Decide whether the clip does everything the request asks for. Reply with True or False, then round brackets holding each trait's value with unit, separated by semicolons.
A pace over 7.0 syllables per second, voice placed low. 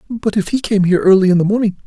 False (7.3 syllables/s; 200 Hz)